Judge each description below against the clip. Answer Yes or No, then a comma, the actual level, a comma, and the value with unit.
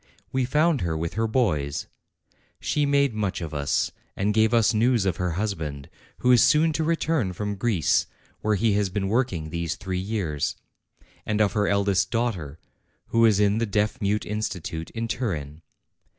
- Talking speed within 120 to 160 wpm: No, average, 175 wpm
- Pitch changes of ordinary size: Yes, average, 4.6 semitones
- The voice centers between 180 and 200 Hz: No, low, 105 Hz